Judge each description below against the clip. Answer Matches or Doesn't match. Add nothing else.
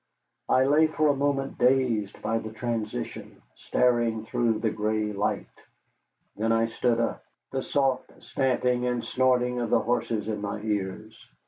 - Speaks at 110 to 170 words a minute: Matches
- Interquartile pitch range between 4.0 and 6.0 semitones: Doesn't match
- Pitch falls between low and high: Doesn't match